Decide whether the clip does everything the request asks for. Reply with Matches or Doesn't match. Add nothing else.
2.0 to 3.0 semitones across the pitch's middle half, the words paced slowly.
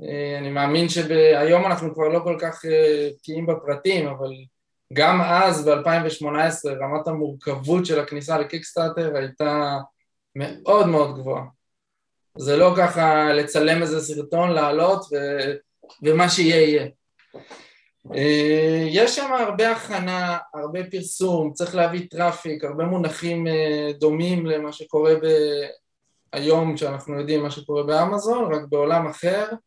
Doesn't match